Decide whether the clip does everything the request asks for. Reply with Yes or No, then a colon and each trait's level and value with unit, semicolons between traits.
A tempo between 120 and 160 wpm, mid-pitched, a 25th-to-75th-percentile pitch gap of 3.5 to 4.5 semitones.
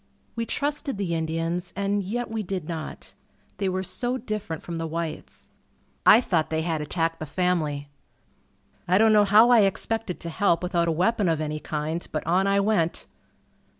No: average, 180 wpm; medium, 180 Hz; average, 4.1 semitones